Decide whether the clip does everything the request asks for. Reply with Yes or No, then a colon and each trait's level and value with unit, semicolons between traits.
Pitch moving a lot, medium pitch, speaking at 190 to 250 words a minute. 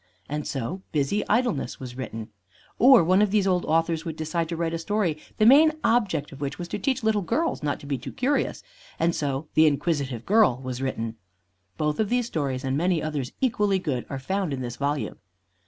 Yes: wide, 6.6 semitones; medium, 160 Hz; fast, 205 wpm